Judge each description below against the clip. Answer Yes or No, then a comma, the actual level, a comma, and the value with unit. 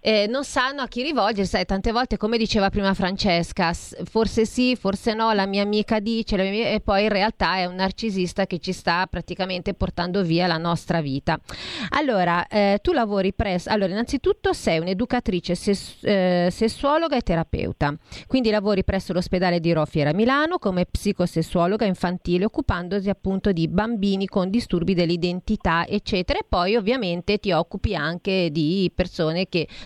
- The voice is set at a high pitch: Yes, high, 195 Hz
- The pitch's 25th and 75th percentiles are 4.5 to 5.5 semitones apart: No, average, 3.6 semitones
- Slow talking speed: No, average, 165 wpm